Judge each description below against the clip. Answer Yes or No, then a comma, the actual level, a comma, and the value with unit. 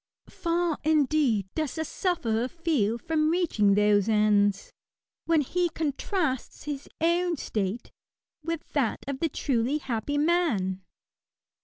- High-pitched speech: Yes, very high, 290 Hz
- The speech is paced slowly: Yes, slow, 120 wpm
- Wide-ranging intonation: Yes, wide, 6.9 semitones